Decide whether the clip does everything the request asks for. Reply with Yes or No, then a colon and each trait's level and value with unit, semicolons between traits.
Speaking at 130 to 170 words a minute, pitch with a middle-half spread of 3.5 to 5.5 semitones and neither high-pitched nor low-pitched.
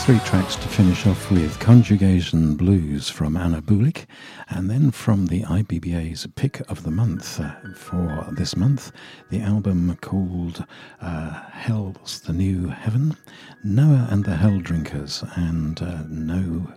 No: average, 140 wpm; average, 4.6 semitones; very low, 95 Hz